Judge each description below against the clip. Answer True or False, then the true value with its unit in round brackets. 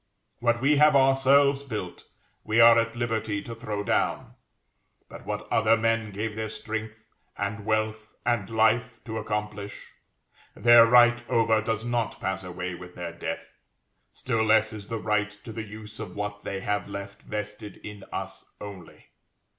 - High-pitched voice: False (110 Hz)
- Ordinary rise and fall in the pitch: False (2.0 semitones)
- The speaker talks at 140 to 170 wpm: True (160 wpm)